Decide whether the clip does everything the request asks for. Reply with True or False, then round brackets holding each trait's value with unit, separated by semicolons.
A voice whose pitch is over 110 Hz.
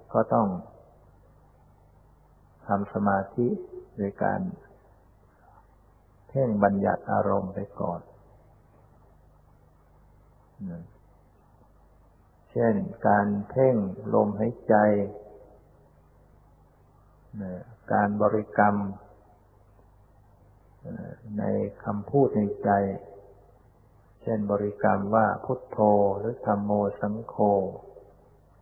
False (105 Hz)